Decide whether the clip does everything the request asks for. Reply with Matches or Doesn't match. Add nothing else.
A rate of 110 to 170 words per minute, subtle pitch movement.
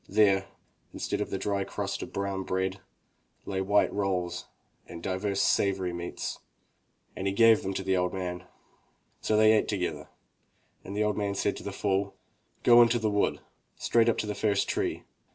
Doesn't match